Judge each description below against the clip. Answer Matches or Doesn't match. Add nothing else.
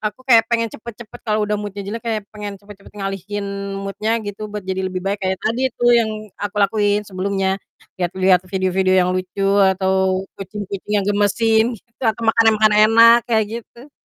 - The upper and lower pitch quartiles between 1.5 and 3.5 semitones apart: Matches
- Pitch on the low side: Doesn't match